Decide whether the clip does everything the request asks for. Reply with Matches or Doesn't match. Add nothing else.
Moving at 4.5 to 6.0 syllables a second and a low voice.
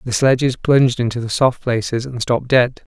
Matches